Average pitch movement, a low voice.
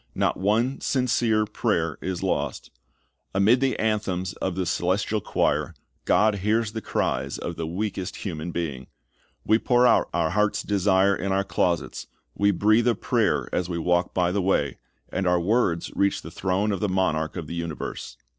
Yes: average, 3.6 semitones; very low, 95 Hz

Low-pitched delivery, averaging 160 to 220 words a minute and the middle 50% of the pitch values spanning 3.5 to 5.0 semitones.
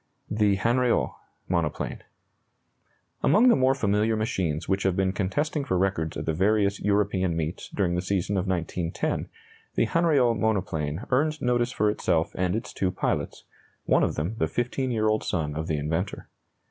Yes: low, 100 Hz; average, 165 wpm; average, 4.6 semitones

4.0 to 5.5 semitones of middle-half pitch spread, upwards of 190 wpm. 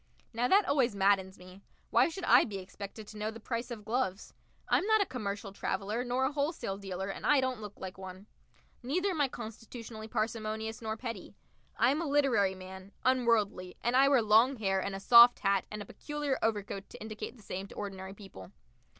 Yes: average, 4.3 semitones; average, 200 wpm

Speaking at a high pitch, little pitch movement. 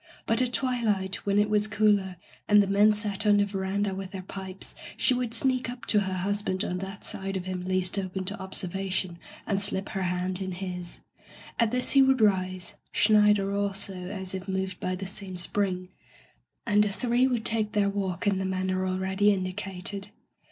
Yes: high, 195 Hz; narrow, 1.8 semitones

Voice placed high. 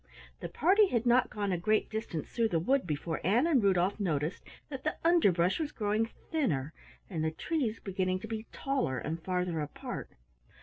Yes: high, 205 Hz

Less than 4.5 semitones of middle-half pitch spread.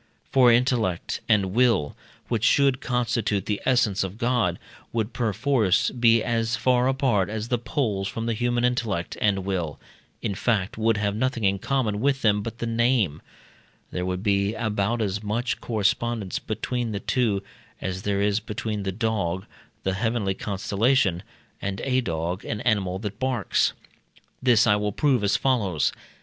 Yes: average, 3.6 semitones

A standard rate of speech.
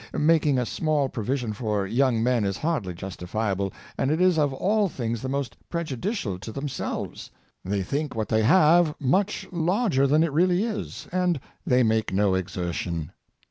Yes: average, 170 wpm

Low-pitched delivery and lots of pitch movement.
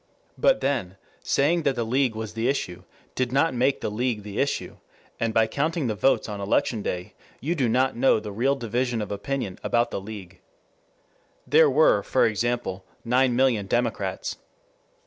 No: low, 120 Hz; average, 4.1 semitones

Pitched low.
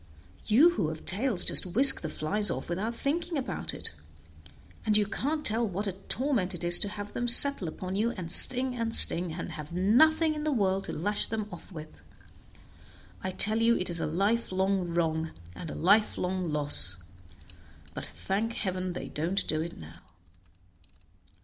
No: high, 195 Hz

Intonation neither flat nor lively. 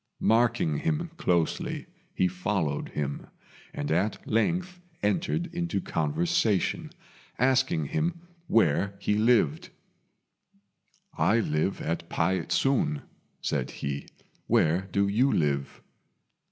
No: wide, 7.4 semitones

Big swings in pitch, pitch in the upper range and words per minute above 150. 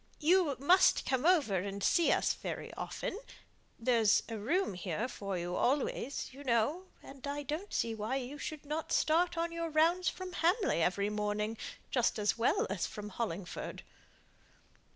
Yes: wide, 7.6 semitones; very high, 260 Hz; average, 160 wpm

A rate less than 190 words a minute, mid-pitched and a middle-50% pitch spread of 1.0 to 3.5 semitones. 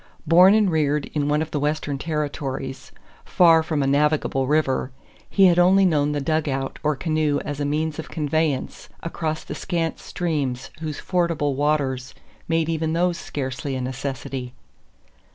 Yes: average, 155 wpm; medium, 150 Hz; average, 2.7 semitones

